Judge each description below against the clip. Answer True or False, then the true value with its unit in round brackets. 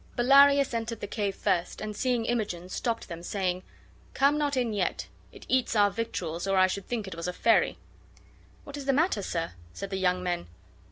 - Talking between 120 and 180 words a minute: False (205 wpm)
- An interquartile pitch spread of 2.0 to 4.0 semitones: False (5.1 semitones)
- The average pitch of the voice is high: True (210 Hz)